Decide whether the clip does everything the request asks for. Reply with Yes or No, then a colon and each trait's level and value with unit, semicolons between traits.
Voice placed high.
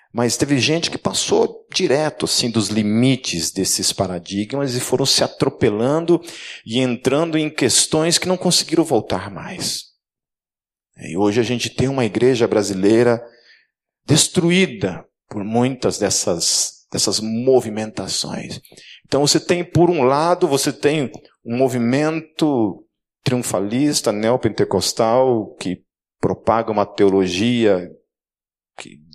No: low, 125 Hz